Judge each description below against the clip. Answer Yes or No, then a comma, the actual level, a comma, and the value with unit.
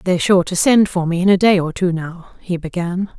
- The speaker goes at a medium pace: No, fast, 265 wpm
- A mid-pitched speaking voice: Yes, medium, 180 Hz